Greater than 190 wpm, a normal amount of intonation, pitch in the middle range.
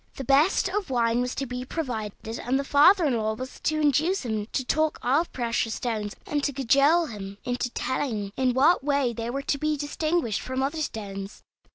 No: average, 200 wpm; average, 4.3 semitones; very high, 260 Hz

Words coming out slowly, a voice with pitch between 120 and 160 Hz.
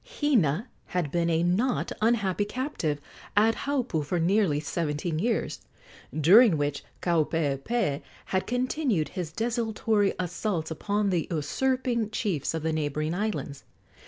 No: slow, 125 wpm; medium, 185 Hz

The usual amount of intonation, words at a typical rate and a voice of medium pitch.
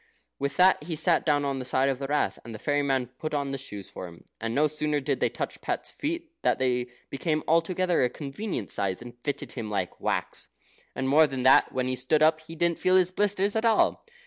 No: average, 4.5 semitones; fast, 235 wpm; medium, 145 Hz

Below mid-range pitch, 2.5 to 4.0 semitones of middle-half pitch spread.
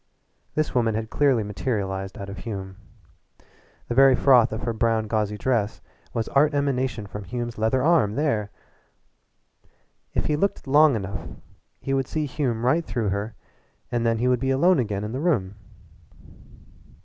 No: low, 115 Hz; average, 4.4 semitones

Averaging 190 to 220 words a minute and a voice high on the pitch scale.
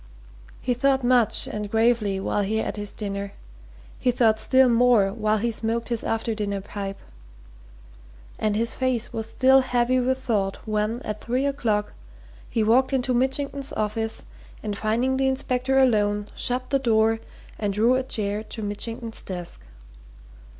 No: average, 155 wpm; high, 225 Hz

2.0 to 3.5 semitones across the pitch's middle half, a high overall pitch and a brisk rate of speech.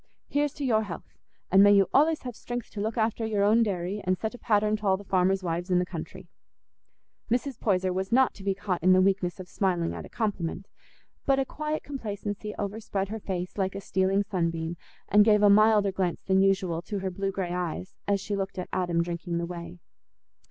Yes: average, 2.8 semitones; high, 195 Hz; fast, 220 wpm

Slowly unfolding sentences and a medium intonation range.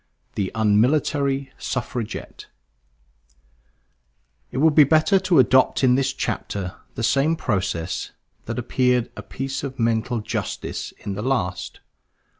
Yes: slow, 120 wpm; average, 3.9 semitones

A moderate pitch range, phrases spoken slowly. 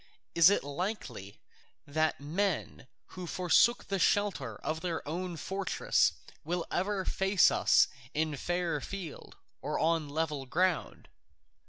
Yes: average, 3.7 semitones; slow, 120 wpm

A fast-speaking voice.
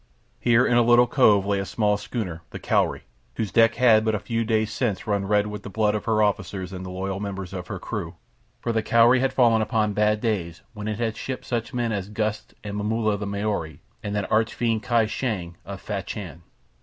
Yes: fast, 220 wpm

